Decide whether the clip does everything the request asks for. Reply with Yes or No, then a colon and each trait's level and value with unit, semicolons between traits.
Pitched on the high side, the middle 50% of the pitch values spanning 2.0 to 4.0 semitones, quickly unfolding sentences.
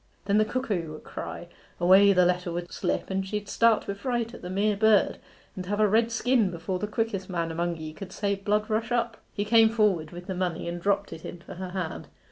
Yes: high, 195 Hz; average, 3.3 semitones; fast, 230 wpm